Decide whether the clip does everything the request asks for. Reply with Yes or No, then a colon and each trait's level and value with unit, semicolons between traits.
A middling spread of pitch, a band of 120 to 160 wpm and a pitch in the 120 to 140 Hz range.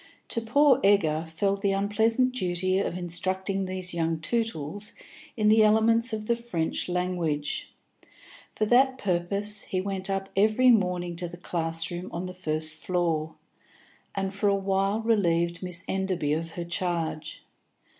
No: average, 3.4 semitones; average, 150 wpm; medium, 185 Hz